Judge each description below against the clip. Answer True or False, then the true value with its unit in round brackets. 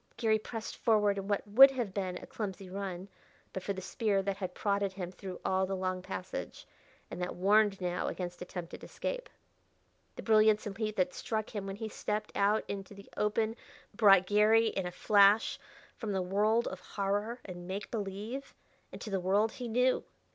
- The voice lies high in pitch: True (200 Hz)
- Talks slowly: False (185 wpm)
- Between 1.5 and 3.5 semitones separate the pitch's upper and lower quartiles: True (2.4 semitones)